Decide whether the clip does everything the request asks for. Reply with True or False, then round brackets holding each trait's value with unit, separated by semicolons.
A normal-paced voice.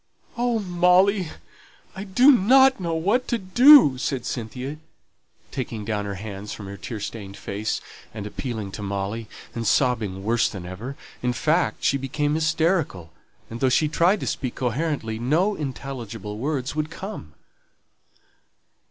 True (145 wpm)